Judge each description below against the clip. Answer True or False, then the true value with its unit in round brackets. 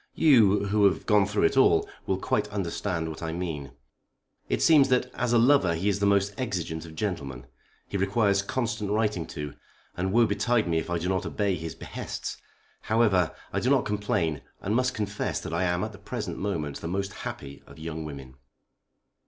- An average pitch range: True (4.4 semitones)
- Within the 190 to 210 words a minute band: True (195 wpm)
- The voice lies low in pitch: True (100 Hz)